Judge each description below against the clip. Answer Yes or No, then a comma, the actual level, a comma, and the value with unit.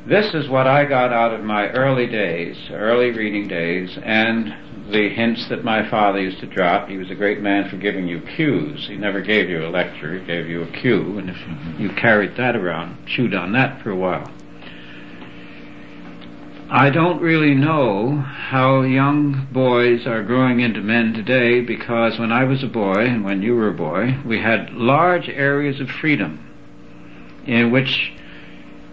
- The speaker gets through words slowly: No, average, 180 wpm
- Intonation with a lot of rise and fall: Yes, wide, 5.8 semitones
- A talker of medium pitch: No, low, 115 Hz